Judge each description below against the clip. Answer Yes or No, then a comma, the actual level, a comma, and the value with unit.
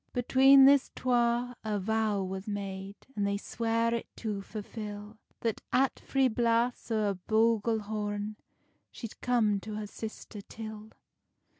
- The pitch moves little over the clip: Yes, narrow, 2.2 semitones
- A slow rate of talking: Yes, slow, 130 wpm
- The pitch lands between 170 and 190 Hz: No, high, 220 Hz